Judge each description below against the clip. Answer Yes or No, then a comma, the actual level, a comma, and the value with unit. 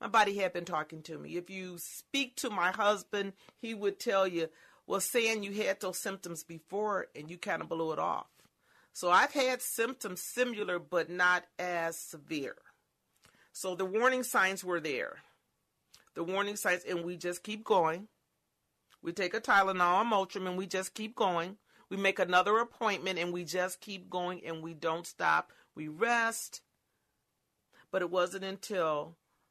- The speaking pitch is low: No, high, 190 Hz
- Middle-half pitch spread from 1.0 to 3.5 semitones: Yes, average, 3.2 semitones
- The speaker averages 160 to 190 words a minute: Yes, average, 170 wpm